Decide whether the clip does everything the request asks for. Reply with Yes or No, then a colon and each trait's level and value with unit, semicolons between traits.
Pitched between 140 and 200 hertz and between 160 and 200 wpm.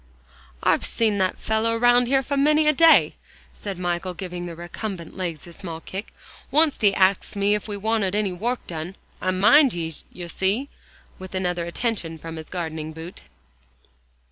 Yes: high, 190 Hz; average, 170 wpm